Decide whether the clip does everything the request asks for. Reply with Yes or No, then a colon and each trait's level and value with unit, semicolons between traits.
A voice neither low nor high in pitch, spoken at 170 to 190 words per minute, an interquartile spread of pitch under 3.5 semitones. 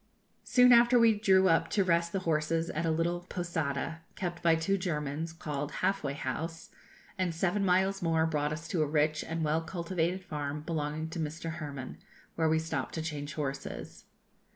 Yes: medium, 165 Hz; average, 180 wpm; average, 2.7 semitones